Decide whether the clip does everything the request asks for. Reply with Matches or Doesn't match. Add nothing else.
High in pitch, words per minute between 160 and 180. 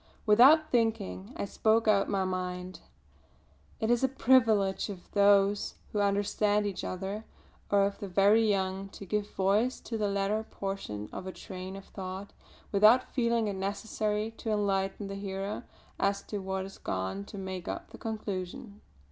Matches